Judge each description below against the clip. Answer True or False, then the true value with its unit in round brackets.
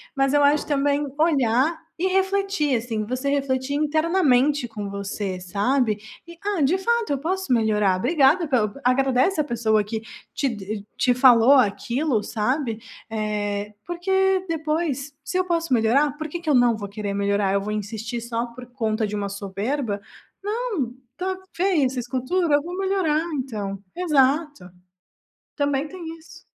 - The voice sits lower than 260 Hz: False (265 Hz)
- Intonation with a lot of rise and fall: True (6.4 semitones)